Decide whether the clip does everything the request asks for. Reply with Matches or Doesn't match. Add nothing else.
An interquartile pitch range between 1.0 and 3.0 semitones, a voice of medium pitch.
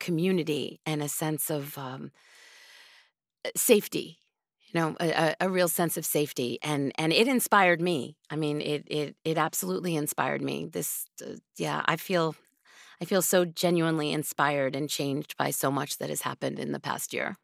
Matches